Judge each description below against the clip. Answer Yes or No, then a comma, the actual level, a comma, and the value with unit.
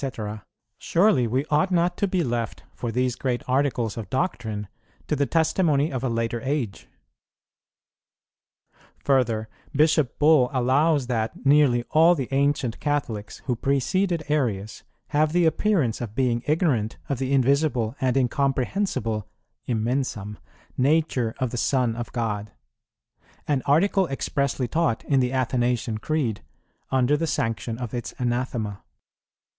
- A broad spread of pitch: No, average, 4.1 semitones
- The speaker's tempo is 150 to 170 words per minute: No, slow, 135 wpm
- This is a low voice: Yes, low, 130 Hz